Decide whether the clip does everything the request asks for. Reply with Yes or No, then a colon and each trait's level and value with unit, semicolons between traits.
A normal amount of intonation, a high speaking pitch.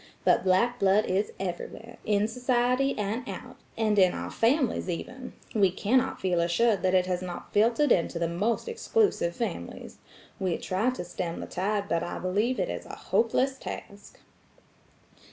Yes: average, 4.7 semitones; high, 205 Hz